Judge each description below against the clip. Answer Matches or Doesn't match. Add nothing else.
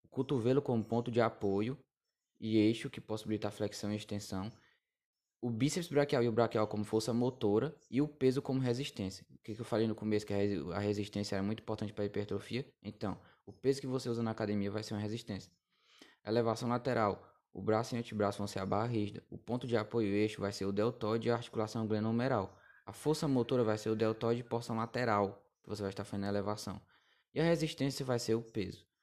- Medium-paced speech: Doesn't match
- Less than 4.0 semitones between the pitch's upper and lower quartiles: Matches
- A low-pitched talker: Matches